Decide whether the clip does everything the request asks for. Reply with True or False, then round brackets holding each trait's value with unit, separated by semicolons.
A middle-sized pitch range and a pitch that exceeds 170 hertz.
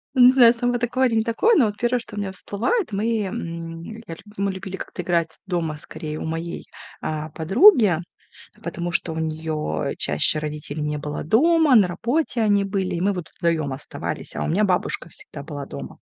False (6.3 semitones; 185 Hz)